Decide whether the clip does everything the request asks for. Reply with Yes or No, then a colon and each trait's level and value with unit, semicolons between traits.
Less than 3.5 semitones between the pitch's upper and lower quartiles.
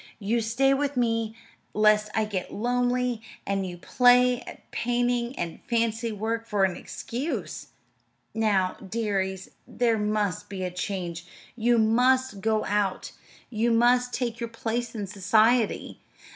Yes: average, 3.1 semitones